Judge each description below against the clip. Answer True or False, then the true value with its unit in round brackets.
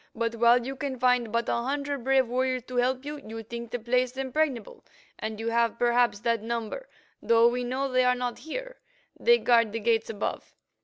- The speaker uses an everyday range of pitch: False (2.1 semitones)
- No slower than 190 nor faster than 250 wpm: True (200 wpm)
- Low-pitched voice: False (245 Hz)